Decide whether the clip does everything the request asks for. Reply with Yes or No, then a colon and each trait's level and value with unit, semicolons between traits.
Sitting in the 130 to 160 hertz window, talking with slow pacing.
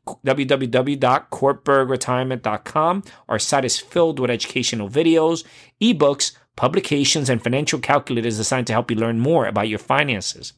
Yes: low, 135 Hz; slow, 125 wpm